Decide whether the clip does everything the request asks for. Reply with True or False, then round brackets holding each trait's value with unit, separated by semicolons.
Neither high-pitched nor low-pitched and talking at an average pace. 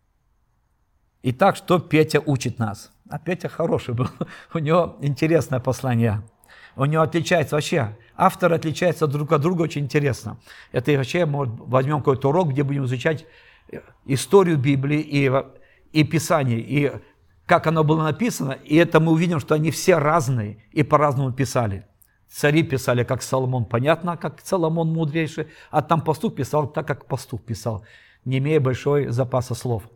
True (145 Hz; 150 wpm)